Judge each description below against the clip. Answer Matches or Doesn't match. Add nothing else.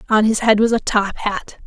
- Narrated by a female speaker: Matches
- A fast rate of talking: Matches